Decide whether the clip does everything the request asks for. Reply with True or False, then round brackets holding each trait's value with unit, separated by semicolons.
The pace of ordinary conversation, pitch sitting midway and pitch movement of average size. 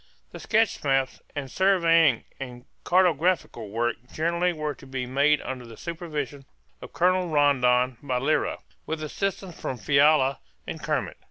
True (145 wpm; 145 Hz; 4.5 semitones)